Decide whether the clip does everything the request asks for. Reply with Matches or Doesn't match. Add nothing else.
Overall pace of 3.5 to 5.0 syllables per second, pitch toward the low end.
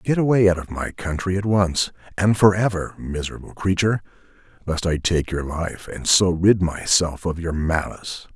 Matches